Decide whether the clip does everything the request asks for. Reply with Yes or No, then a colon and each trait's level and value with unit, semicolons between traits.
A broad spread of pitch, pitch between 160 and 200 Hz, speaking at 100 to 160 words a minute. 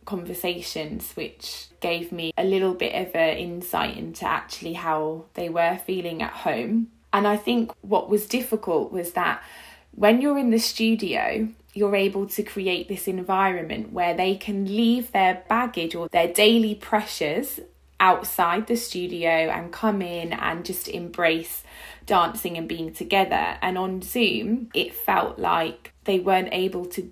No: average, 3.6 semitones; high, 190 Hz; average, 155 wpm